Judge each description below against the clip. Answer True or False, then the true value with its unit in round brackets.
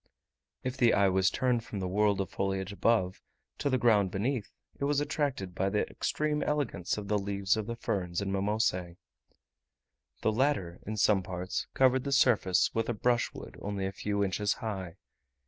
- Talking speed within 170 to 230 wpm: True (180 wpm)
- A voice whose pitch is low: True (105 Hz)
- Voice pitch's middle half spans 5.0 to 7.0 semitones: False (4.0 semitones)